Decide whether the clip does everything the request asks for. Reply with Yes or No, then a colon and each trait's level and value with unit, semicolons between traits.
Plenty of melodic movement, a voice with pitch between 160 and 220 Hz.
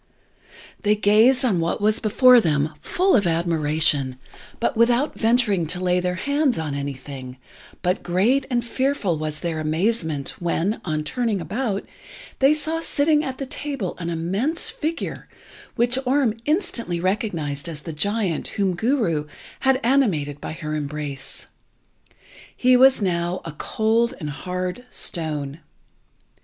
Yes: wide, 7.7 semitones; high, 190 Hz